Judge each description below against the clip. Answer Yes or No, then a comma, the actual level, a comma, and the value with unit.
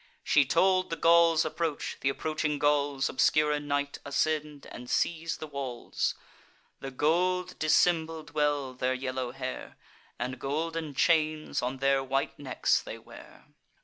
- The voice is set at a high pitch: No, medium, 150 Hz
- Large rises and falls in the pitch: No, average, 2.9 semitones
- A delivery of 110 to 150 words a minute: Yes, average, 140 wpm